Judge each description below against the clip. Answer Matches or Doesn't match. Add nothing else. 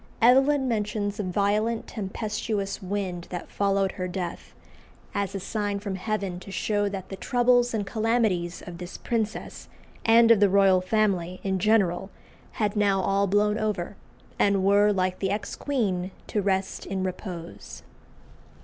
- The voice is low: Doesn't match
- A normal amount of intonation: Doesn't match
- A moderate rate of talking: Matches